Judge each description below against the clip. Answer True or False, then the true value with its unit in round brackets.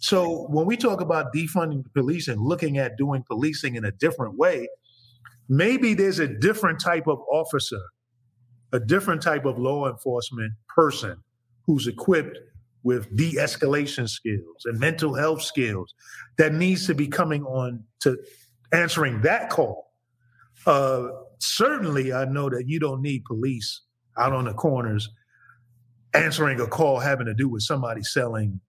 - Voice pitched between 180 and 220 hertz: False (130 Hz)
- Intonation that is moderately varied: True (4.5 semitones)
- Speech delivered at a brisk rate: False (155 wpm)